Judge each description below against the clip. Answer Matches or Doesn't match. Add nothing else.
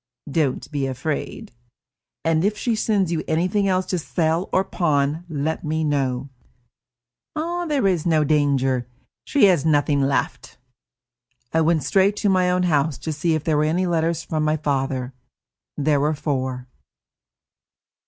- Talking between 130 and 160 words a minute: Matches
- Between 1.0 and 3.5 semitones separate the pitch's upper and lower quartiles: Doesn't match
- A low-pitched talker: Doesn't match